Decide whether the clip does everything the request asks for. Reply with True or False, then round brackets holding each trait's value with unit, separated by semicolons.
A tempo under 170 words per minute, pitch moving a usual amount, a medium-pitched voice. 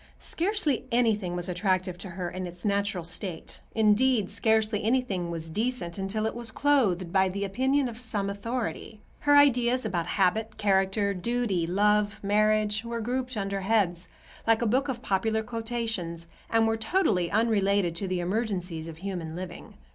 False (155 wpm; 3.8 semitones; 210 Hz)